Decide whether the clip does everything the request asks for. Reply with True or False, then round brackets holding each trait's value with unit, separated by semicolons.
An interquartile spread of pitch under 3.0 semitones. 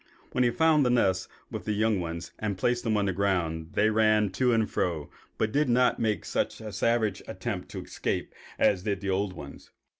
False (3.7 semitones)